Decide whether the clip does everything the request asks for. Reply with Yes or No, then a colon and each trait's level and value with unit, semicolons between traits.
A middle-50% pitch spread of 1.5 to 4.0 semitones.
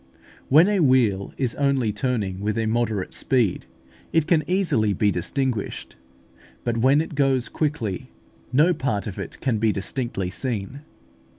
No: average, 5.0 semitones